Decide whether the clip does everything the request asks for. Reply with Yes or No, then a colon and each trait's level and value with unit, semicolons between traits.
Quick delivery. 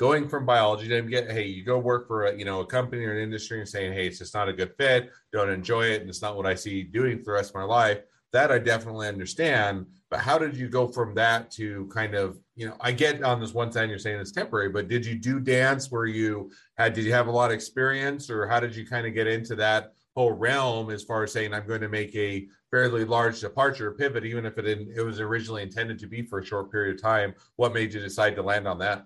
Yes: fast, 275 wpm